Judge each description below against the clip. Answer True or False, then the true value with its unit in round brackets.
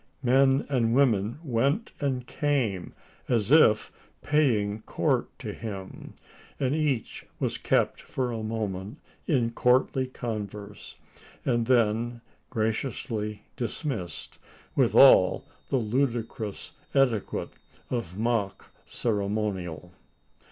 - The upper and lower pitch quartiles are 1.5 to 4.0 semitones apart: True (3.7 semitones)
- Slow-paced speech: True (100 wpm)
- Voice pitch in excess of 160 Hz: False (115 Hz)